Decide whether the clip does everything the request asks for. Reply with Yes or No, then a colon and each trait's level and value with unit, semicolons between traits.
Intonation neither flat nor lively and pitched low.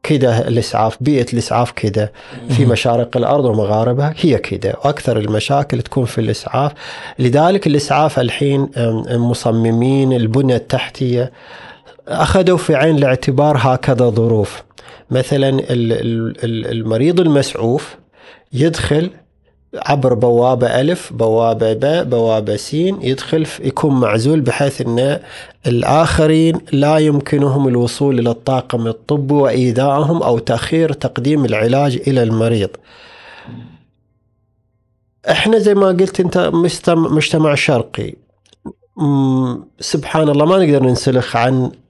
Yes: average, 4.1 semitones; low, 130 Hz